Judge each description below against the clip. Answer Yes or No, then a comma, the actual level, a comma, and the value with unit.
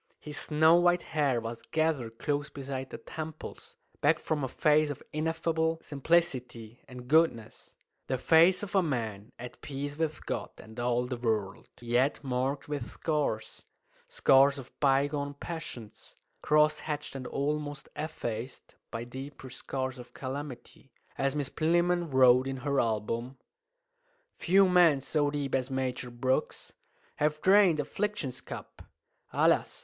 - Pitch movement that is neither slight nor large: Yes, average, 3.8 semitones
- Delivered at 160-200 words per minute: No, average, 140 wpm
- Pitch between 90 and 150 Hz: Yes, medium, 140 Hz